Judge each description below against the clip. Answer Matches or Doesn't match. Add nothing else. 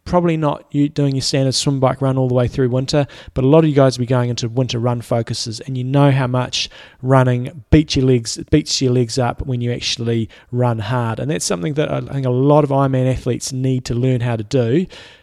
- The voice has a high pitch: Doesn't match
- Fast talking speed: Matches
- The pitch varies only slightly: Matches